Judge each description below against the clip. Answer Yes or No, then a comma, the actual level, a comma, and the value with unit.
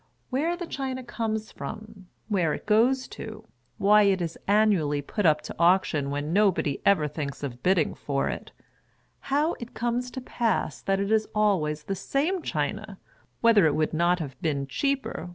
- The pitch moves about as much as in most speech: No, wide, 6.9 semitones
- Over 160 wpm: Yes, average, 185 wpm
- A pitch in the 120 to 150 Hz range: No, high, 195 Hz